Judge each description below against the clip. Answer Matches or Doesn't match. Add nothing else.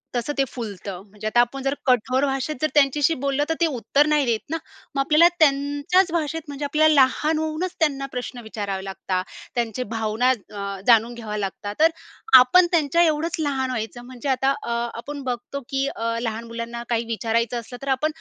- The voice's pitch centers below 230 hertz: Doesn't match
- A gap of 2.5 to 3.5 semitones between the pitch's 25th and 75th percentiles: Doesn't match